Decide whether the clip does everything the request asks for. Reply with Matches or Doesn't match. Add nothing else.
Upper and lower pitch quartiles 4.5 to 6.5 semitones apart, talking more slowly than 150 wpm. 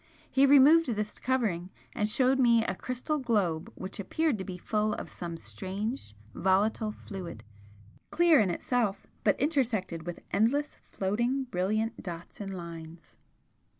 Matches